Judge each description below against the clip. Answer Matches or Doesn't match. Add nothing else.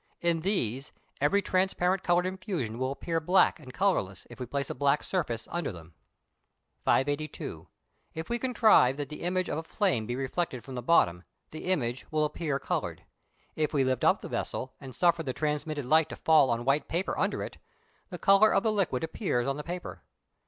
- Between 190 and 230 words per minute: Matches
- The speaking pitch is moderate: Matches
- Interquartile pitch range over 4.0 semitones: Matches